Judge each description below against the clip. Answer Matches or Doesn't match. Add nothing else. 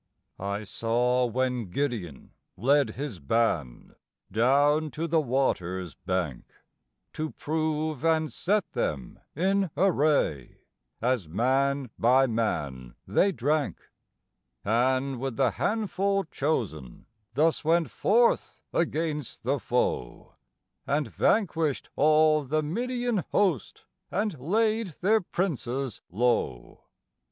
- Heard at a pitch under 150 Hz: Matches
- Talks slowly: Matches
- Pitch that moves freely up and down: Matches